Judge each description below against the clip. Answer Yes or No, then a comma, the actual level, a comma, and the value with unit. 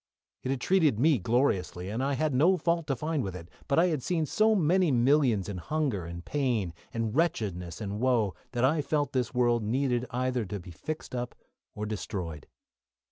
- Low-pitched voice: Yes, low, 125 Hz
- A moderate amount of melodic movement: No, wide, 6.3 semitones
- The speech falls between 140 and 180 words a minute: No, average, 190 wpm